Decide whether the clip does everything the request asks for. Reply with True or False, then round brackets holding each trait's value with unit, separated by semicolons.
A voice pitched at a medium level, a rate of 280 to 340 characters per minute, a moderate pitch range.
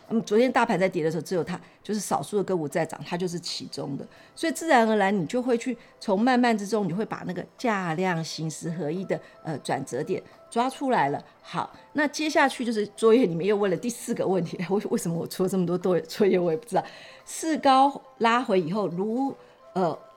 False (205 Hz; 325 characters per minute; 5.0 semitones)